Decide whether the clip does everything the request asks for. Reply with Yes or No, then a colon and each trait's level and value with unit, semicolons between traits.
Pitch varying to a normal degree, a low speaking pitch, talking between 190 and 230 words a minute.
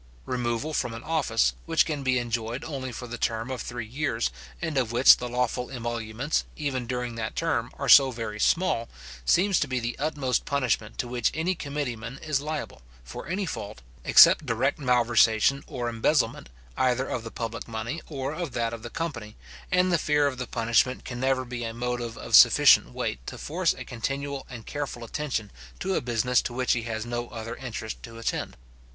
Yes: average, 3.4 semitones; low, 125 Hz; average, 195 wpm